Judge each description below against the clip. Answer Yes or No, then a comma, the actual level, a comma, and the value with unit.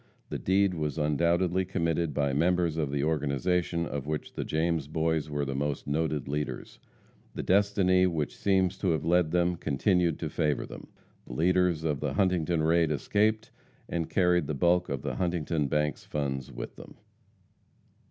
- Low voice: Yes, very low, 80 Hz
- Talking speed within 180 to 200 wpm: No, average, 165 wpm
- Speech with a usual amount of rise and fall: Yes, average, 3.2 semitones